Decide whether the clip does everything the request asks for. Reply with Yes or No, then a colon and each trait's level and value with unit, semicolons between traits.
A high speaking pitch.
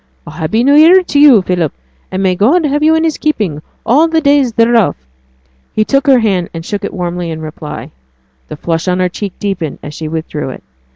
Yes: high, 200 Hz